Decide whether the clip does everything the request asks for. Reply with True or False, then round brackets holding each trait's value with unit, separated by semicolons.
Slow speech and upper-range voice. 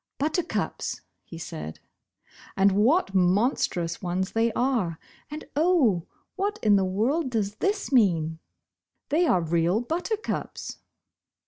True (115 wpm; 215 Hz)